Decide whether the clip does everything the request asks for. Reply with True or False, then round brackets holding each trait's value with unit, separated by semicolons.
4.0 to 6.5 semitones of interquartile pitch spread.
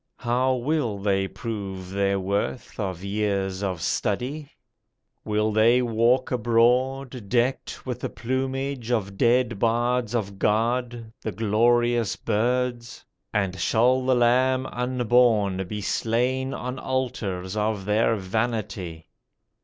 False (3.6 semitones)